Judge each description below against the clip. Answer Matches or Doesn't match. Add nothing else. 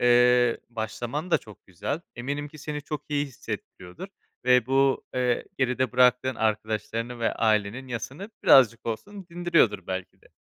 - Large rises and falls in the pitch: Doesn't match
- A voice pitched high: Doesn't match